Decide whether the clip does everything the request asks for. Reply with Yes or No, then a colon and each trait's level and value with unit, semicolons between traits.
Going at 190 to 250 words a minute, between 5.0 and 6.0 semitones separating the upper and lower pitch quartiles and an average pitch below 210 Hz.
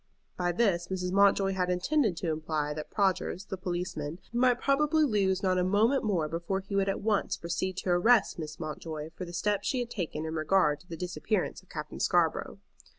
No: average, 200 wpm; average, 3.2 semitones; medium, 185 Hz